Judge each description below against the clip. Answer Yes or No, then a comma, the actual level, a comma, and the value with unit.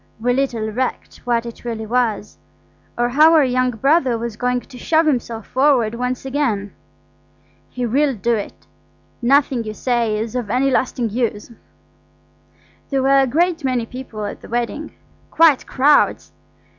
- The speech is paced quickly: No, average, 150 wpm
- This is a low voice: No, very high, 250 Hz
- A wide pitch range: No, average, 2.9 semitones